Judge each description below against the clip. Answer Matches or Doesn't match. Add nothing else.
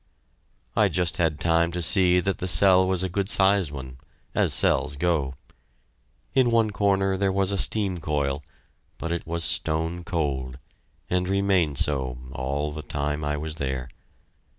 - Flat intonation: Doesn't match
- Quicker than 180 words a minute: Doesn't match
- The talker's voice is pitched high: Doesn't match